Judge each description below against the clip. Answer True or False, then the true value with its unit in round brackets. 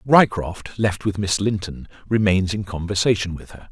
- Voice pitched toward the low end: True (100 Hz)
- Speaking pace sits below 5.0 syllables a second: True (4.7 syllables/s)